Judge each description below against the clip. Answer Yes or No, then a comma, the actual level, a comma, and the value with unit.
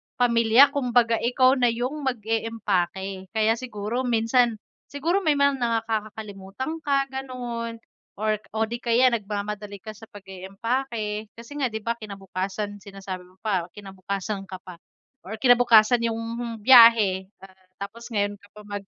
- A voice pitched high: Yes, high, 220 Hz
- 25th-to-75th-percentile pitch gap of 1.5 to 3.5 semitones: Yes, average, 3.2 semitones